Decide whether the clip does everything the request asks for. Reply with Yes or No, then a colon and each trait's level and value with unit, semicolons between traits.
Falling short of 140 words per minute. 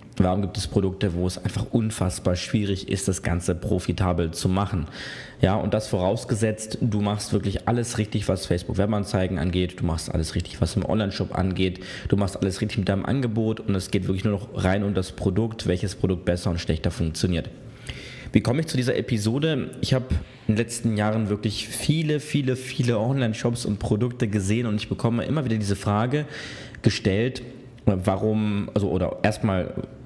No: average, 180 wpm